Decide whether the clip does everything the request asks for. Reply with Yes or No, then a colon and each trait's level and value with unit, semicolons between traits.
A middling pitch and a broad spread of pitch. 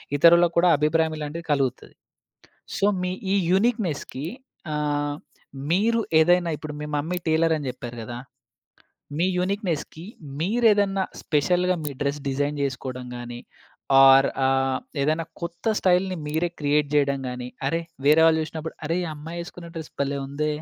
No: medium, 155 Hz; average, 3.7 semitones